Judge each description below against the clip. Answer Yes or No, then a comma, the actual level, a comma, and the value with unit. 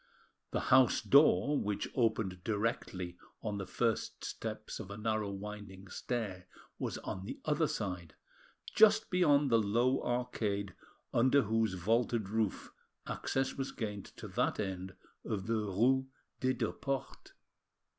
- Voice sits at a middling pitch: No, low, 110 Hz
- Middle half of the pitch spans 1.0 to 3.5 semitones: No, average, 4.0 semitones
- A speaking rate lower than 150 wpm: Yes, slow, 135 wpm